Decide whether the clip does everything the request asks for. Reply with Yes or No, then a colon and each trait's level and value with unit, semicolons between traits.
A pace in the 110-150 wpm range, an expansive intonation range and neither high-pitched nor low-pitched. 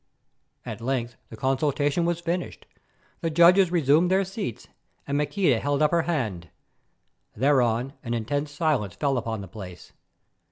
Yes: average, 145 wpm; wide, 6.2 semitones; medium, 145 Hz